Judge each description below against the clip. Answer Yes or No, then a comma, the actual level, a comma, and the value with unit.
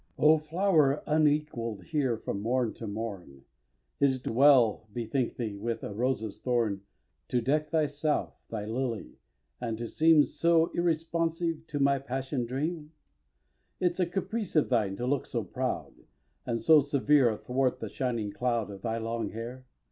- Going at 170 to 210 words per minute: No, average, 155 wpm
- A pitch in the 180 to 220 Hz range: No, low, 130 Hz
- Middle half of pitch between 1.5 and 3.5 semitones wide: No, average, 5.0 semitones